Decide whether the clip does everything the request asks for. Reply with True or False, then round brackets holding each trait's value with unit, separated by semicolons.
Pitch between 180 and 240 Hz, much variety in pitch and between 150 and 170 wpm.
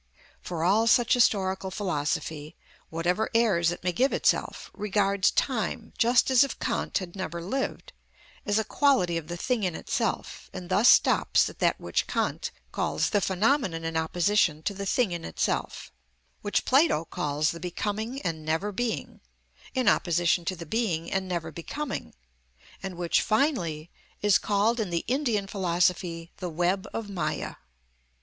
False (190 Hz; 4.4 semitones; 155 wpm)